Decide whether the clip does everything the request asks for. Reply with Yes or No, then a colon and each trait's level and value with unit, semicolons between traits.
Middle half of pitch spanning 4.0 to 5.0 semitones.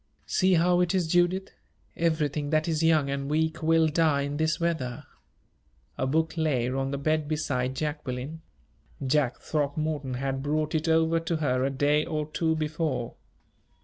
No: narrow, 2.5 semitones